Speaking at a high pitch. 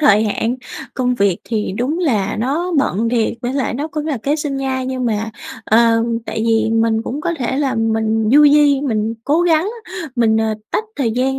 Yes: high, 245 Hz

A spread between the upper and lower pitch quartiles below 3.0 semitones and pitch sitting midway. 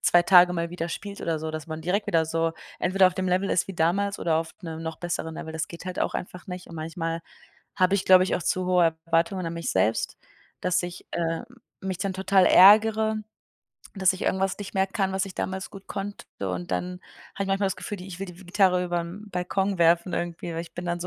Yes: narrow, 2.4 semitones; medium, 180 Hz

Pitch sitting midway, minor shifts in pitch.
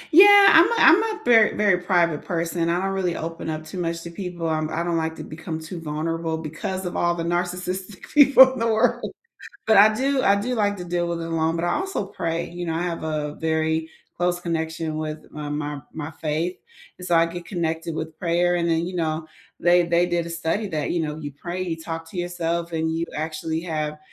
Yes: medium, 170 Hz; narrow, 2.0 semitones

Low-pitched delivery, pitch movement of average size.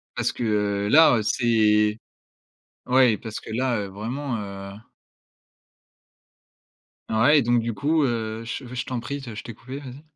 Yes: low, 115 Hz; average, 3.3 semitones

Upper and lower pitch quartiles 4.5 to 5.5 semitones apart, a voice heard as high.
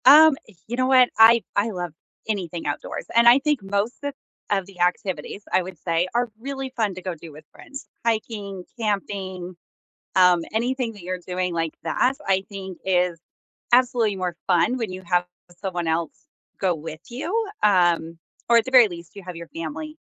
Yes: average, 5.0 semitones; high, 195 Hz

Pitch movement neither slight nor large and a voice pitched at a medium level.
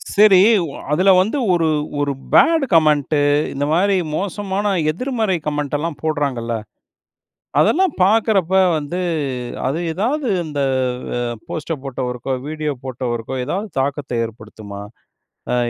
No: wide, 6.4 semitones; medium, 155 Hz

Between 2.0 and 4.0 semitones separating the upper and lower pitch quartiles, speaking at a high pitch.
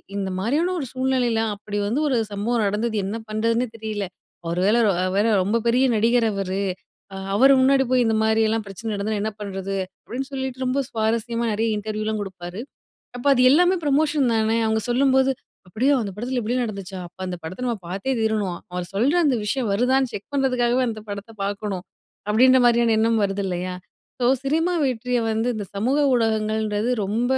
Yes: average, 3.6 semitones; high, 225 Hz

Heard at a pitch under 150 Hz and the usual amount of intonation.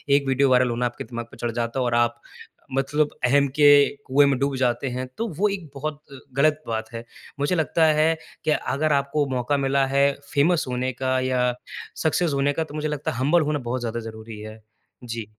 Yes: low, 135 Hz; average, 3.3 semitones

